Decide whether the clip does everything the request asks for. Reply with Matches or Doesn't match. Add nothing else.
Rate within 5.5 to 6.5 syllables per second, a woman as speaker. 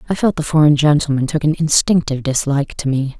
Matches